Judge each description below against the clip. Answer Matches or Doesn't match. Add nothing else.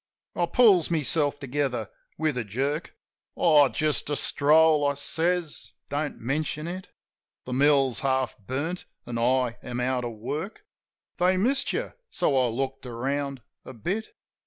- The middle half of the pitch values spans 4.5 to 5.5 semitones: Doesn't match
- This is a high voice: Doesn't match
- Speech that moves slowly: Doesn't match